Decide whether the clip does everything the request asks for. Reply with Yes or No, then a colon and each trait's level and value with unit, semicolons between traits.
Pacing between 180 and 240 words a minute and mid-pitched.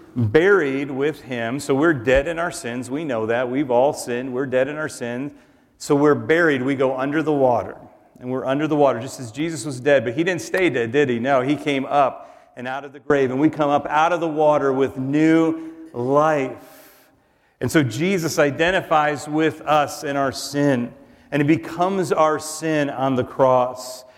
Yes: fast, 205 wpm; medium, 145 Hz